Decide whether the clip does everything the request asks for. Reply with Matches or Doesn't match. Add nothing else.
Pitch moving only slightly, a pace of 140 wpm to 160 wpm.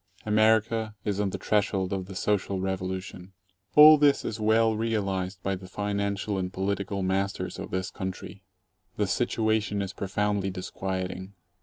Matches